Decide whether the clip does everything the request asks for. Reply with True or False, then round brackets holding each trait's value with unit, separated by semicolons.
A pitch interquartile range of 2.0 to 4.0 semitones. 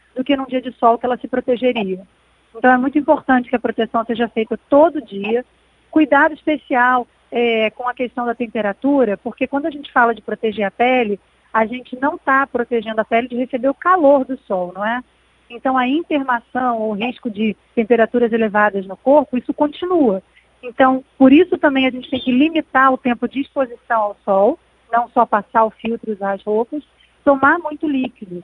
True (3.2 semitones)